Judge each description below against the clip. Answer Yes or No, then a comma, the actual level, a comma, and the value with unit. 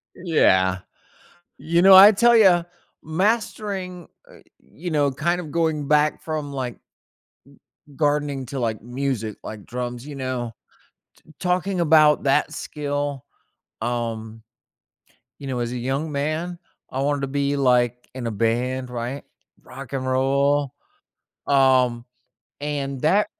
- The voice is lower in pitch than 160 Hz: Yes, medium, 140 Hz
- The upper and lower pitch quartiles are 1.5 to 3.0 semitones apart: No, average, 4.0 semitones